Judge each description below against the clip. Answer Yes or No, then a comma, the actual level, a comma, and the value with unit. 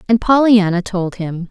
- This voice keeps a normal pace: Yes, average, 160 wpm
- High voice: Yes, high, 200 Hz